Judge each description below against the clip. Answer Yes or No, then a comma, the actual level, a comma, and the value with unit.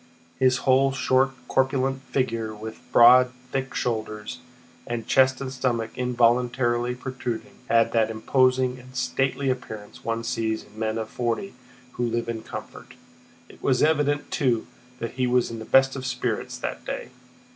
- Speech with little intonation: Yes, narrow, 2.2 semitones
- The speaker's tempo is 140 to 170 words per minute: Yes, average, 155 wpm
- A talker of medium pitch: No, low, 125 Hz